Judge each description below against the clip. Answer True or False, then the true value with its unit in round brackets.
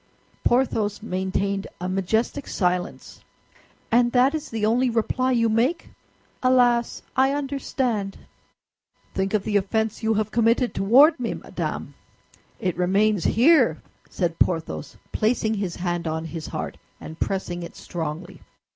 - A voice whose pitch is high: True (215 Hz)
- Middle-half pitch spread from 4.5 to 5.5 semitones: True (4.9 semitones)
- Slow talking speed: True (130 wpm)